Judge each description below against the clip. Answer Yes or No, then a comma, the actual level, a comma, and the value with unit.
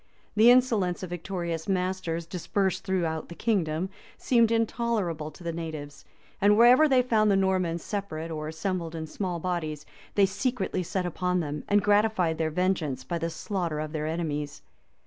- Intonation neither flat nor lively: Yes, average, 4.0 semitones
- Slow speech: No, average, 165 wpm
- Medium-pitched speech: Yes, medium, 180 Hz